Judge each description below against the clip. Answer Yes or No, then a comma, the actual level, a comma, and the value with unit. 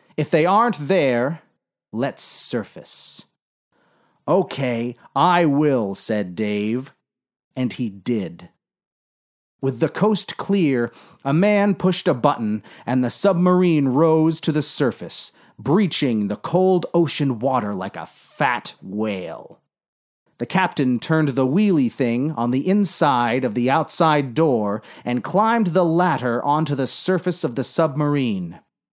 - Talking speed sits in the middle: No, slow, 130 wpm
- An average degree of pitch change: No, wide, 6.5 semitones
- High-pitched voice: No, medium, 145 Hz